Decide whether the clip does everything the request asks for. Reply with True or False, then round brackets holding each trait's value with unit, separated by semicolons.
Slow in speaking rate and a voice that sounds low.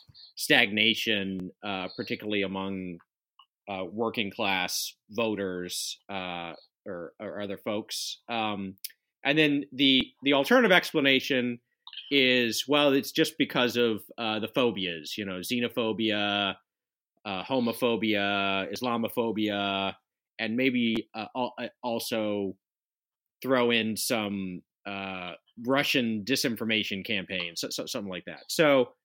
True (105 wpm; 110 Hz)